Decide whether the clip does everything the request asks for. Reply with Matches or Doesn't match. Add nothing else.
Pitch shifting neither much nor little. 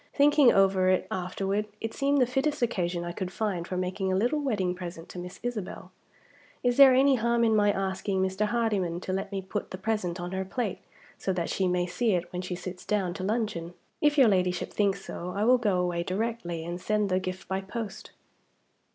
Matches